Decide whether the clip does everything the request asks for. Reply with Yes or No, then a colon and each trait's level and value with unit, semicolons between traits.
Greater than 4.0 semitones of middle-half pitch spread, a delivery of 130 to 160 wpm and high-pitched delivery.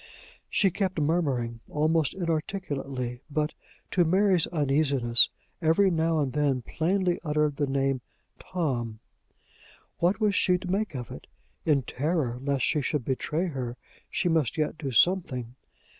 No: average, 4.5 semitones; average, 140 wpm; medium, 150 Hz